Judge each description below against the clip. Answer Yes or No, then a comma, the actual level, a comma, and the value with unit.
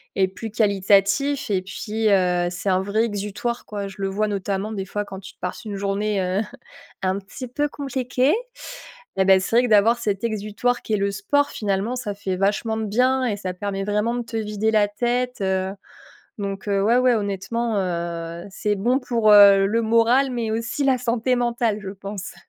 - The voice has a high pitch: Yes, high, 210 Hz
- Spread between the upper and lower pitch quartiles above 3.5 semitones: No, average, 3.1 semitones